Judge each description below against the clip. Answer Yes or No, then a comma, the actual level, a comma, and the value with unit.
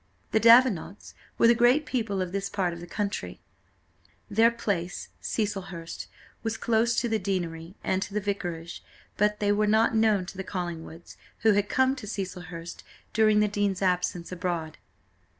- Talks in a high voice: Yes, high, 200 Hz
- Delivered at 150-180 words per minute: Yes, average, 165 wpm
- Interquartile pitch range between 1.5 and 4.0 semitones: Yes, average, 3.7 semitones